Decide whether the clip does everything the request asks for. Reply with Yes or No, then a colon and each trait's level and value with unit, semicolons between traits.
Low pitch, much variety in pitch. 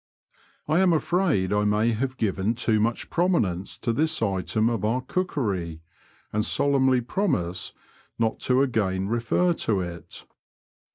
Yes: low, 115 Hz; wide, 5.8 semitones